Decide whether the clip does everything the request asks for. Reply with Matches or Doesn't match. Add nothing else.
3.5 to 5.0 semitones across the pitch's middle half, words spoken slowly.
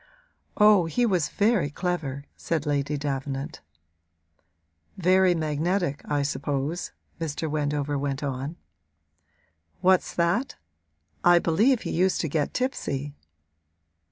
Matches